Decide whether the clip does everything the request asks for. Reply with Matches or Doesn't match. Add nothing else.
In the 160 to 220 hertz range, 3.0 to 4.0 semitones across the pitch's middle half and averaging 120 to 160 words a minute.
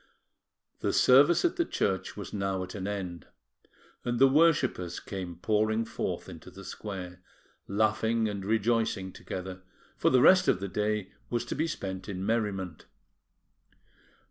Doesn't match